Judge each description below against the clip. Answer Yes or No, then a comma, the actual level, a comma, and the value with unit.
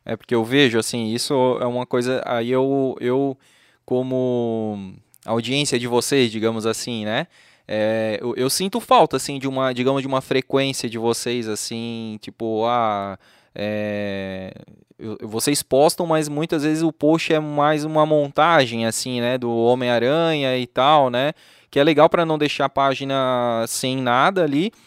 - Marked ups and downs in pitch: No, average, 3.4 semitones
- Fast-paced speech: No, average, 160 wpm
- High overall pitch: No, low, 125 Hz